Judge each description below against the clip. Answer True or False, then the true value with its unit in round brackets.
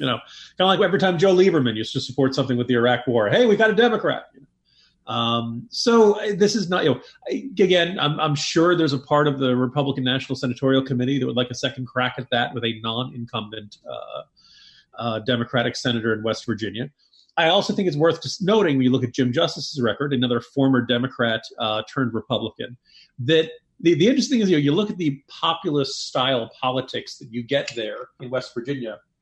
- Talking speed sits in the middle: False (210 wpm)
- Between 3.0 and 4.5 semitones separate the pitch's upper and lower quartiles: False (5.5 semitones)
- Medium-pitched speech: False (130 Hz)